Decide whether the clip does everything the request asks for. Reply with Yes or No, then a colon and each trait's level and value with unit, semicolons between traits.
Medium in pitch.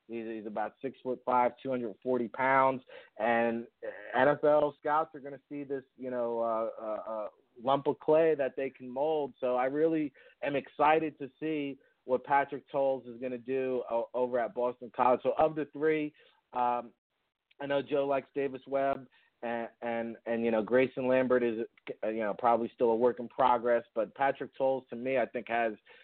No: low, 130 Hz